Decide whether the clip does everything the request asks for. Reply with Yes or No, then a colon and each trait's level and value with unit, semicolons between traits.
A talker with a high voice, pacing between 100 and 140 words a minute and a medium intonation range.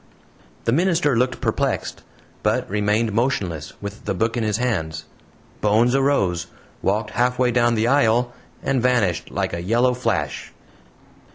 No: low, 115 Hz; slow, 135 wpm; average, 3.7 semitones